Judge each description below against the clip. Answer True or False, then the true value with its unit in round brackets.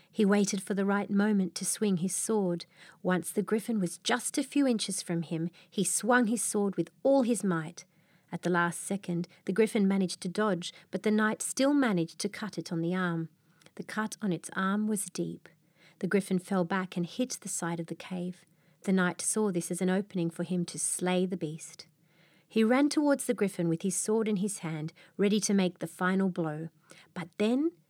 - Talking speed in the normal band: False (210 wpm)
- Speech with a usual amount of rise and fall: True (3.3 semitones)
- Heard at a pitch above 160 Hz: True (185 Hz)